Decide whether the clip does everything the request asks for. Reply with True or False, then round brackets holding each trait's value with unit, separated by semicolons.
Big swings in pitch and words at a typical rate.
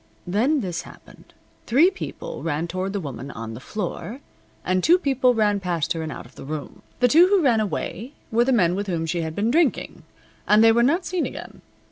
False (7.6 semitones; 215 wpm)